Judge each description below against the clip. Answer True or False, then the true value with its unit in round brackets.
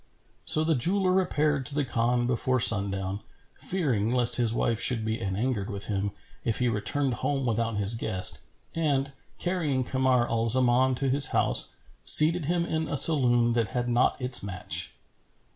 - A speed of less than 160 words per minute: False (165 wpm)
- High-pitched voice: False (125 Hz)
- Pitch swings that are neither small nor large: True (4.0 semitones)